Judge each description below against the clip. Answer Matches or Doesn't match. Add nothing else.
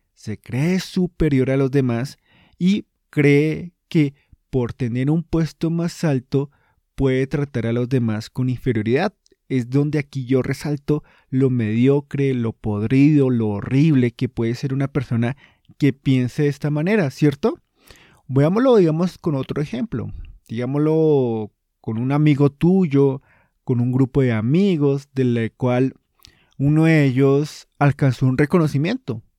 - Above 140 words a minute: Doesn't match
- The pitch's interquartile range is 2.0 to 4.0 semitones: Matches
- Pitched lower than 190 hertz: Matches